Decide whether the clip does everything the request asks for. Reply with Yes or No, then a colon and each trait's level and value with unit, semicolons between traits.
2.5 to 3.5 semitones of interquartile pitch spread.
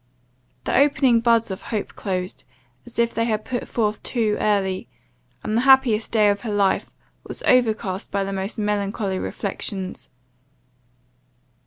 Yes: average, 2.9 semitones